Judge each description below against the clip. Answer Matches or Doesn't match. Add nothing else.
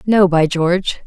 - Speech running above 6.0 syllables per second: Doesn't match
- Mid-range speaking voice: Matches